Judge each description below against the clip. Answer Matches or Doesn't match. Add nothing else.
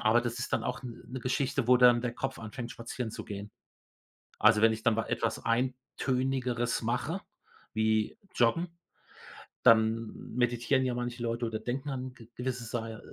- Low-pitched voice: Matches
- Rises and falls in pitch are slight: Matches